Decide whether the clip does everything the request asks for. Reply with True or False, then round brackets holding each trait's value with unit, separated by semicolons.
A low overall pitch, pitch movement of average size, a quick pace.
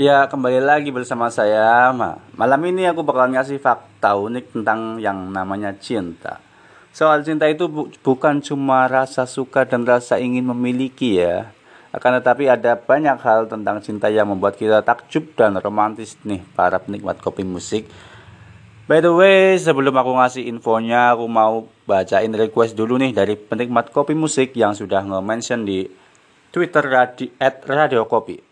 True (120 Hz; 3.9 semitones; 155 wpm)